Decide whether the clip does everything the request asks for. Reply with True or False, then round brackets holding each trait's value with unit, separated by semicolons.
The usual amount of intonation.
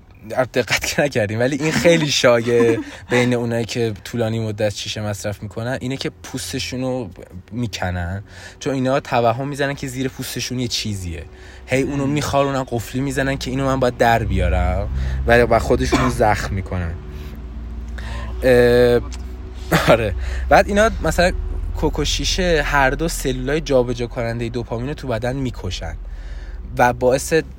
False (6.2 semitones)